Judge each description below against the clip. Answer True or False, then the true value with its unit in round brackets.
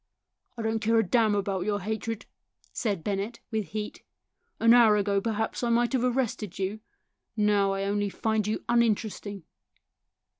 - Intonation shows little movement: True (2.1 semitones)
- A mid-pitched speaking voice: False (215 Hz)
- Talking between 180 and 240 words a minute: False (165 wpm)